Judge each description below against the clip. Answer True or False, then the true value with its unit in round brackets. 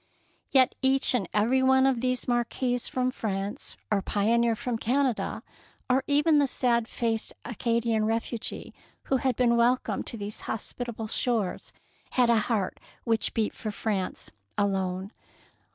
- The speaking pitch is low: False (235 Hz)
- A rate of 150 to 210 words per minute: False (140 wpm)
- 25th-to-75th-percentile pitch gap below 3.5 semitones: True (2.9 semitones)